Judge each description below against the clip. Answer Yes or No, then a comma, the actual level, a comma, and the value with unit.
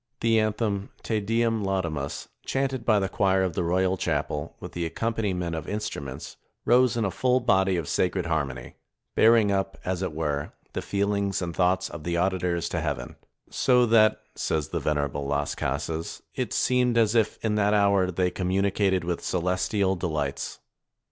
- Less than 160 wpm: No, average, 170 wpm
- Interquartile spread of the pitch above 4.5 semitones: No, average, 4.1 semitones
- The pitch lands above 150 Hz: No, very low, 95 Hz